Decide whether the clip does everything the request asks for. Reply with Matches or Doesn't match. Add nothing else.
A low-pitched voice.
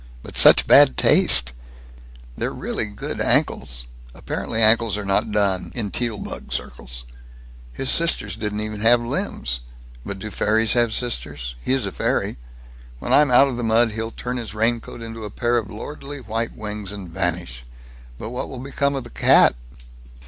Matches